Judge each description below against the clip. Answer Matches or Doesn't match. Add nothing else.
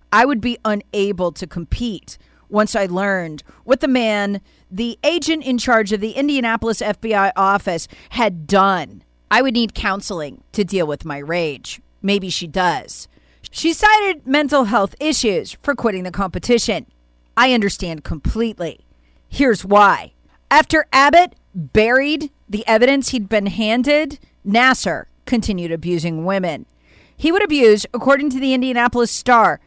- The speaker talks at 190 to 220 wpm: Doesn't match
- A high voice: Matches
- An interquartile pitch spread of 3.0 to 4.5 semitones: Doesn't match